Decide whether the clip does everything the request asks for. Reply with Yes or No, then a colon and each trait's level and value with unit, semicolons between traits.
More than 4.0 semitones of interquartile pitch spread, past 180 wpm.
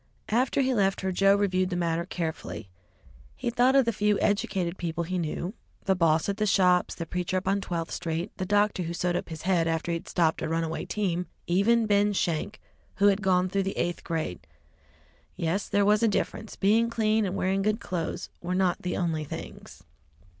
No: average, 3.2 semitones; average, 200 wpm